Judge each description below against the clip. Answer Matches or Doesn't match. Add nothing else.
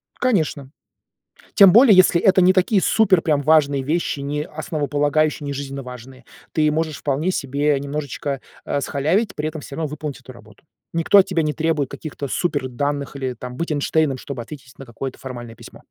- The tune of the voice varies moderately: Matches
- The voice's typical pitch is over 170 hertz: Doesn't match